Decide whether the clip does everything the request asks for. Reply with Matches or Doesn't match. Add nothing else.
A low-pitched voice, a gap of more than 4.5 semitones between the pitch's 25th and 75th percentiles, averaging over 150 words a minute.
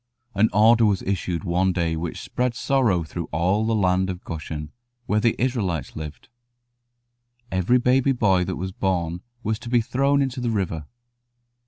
Matches